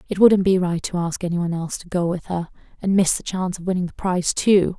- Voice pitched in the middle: Yes, medium, 180 Hz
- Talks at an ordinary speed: No, fast, 275 wpm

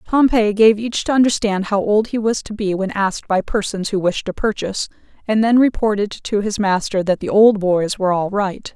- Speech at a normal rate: No, fast, 220 wpm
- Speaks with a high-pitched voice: Yes, high, 205 Hz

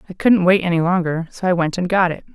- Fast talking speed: Yes, fast, 280 wpm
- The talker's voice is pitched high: No, medium, 175 Hz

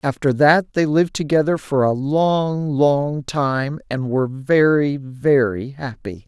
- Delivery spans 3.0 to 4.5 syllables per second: Yes, 3.8 syllables/s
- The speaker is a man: Yes, male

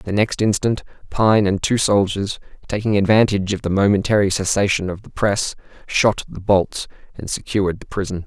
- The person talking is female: No, male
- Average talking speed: Yes, average, 165 wpm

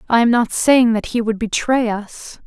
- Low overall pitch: No, high, 230 Hz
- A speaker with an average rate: No, fast, 220 wpm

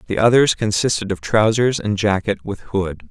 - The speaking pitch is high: No, low, 105 Hz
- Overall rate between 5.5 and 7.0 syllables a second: No, 5.0 syllables/s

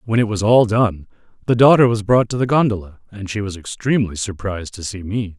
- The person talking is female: No, male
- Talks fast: Yes, fast, 225 wpm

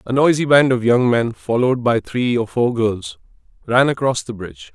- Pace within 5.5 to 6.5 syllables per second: No, 5.0 syllables/s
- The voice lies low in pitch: Yes, low, 125 Hz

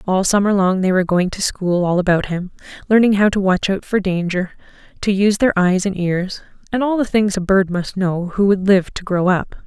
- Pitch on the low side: No, high, 190 Hz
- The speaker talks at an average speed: No, fast, 235 wpm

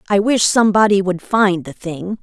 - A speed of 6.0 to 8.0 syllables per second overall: No, 5.0 syllables/s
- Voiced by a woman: Yes, female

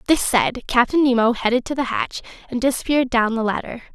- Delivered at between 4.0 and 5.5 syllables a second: No, 5.9 syllables/s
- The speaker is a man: No, female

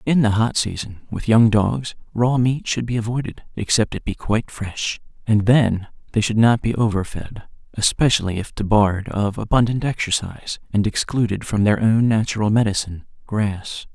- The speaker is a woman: No, male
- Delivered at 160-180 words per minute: Yes, average, 170 wpm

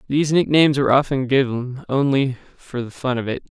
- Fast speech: No, average, 185 wpm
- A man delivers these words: Yes, male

